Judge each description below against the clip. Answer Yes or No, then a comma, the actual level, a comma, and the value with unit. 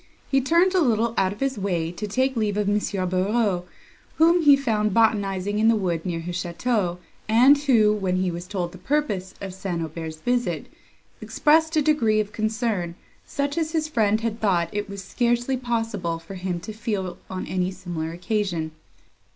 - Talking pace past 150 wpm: Yes, average, 185 wpm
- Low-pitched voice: No, high, 210 Hz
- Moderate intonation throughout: Yes, average, 4.8 semitones